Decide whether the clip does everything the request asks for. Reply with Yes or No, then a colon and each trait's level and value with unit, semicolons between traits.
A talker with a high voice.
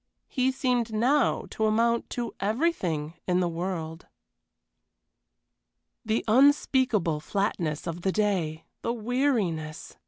Yes: high, 215 Hz